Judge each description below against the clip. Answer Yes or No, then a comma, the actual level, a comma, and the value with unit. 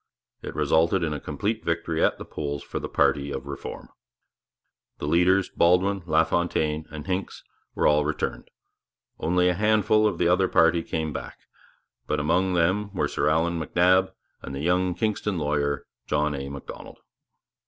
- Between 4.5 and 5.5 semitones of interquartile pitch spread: No, average, 3.5 semitones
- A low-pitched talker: Yes, very low, 85 Hz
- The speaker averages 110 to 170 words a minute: Yes, average, 160 wpm